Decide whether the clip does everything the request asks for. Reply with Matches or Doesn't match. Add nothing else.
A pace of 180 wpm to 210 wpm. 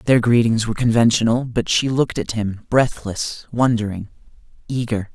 Doesn't match